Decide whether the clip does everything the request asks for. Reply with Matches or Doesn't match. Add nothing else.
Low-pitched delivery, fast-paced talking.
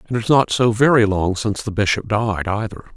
Matches